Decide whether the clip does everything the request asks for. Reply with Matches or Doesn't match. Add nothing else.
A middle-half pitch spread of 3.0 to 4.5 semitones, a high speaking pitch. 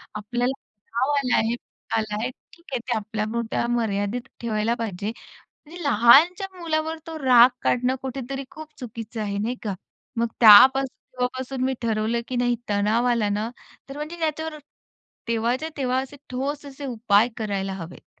Matches